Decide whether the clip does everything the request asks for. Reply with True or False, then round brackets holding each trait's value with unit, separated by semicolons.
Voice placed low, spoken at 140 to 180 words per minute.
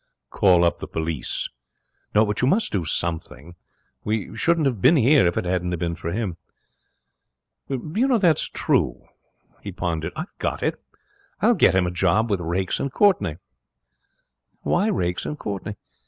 True (100 Hz; 155 wpm)